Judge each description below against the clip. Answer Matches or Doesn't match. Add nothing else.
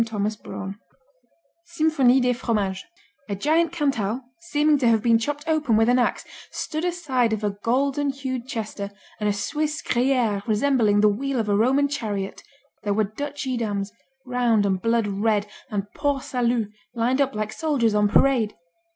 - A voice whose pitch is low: Doesn't match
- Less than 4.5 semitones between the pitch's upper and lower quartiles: Doesn't match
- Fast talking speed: Doesn't match